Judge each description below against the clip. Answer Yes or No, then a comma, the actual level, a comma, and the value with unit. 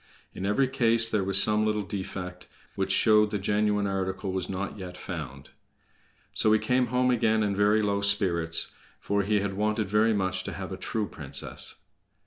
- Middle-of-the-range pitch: No, low, 100 Hz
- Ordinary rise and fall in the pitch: No, narrow, 2.3 semitones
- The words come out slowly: No, average, 180 wpm